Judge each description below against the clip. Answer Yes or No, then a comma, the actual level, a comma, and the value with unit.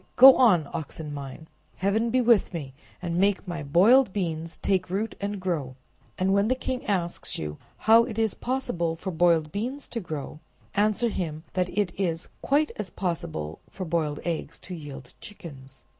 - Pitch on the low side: No, medium, 180 Hz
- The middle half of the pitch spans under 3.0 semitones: No, average, 5.0 semitones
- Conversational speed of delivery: Yes, average, 175 wpm